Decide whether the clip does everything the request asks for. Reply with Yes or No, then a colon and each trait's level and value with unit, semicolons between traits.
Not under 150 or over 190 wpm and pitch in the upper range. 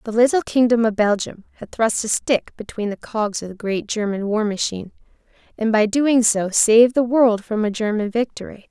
No: average, 200 wpm; high, 220 Hz